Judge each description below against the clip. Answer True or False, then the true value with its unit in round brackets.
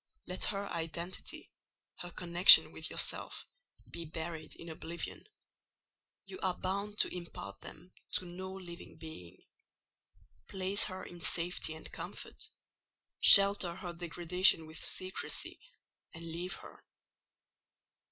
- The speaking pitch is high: False (175 Hz)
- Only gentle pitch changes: True (2.0 semitones)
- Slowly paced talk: True (115 wpm)